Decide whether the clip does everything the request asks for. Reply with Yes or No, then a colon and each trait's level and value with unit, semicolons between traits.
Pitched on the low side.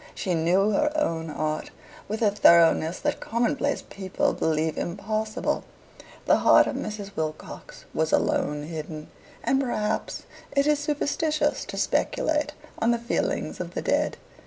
No: high, 205 Hz